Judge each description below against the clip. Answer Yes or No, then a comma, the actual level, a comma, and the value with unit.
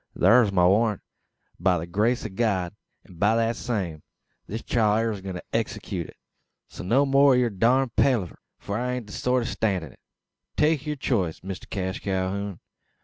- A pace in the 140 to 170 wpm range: No, average, 190 wpm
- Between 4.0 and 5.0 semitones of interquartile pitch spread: Yes, average, 4.4 semitones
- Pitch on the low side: Yes, low, 105 Hz